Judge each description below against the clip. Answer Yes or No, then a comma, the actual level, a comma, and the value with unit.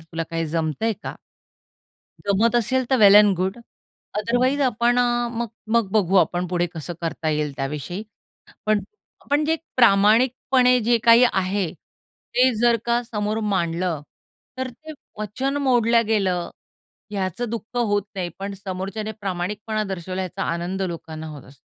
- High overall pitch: Yes, high, 205 Hz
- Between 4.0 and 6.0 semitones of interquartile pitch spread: Yes, average, 5.0 semitones